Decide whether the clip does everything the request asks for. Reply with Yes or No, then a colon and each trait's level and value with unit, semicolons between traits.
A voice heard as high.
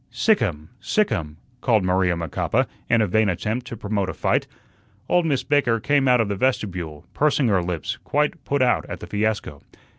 No: low, 110 Hz